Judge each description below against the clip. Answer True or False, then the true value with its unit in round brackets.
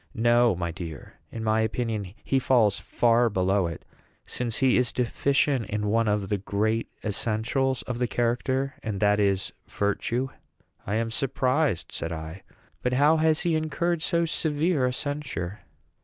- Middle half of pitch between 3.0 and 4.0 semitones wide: False (4.6 semitones)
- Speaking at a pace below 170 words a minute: True (155 wpm)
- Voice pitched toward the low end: True (115 Hz)